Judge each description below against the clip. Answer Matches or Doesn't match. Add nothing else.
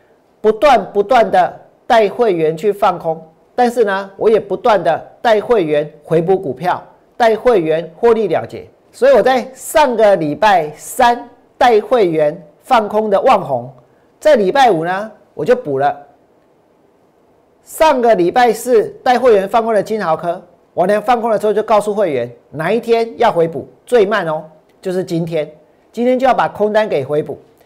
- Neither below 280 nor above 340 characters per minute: Doesn't match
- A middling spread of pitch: Doesn't match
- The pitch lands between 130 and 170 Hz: Doesn't match